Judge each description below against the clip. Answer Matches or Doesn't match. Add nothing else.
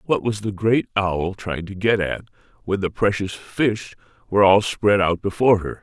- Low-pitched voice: Matches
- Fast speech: Doesn't match